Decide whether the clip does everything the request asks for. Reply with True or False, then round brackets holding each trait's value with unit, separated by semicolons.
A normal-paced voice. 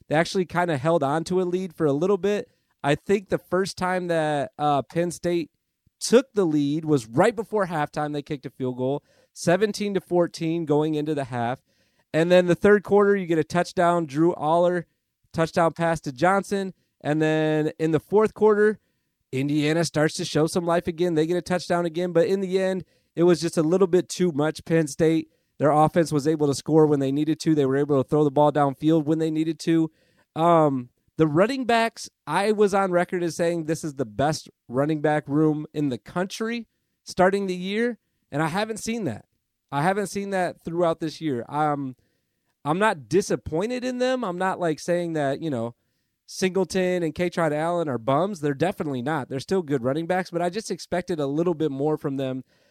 False (210 wpm)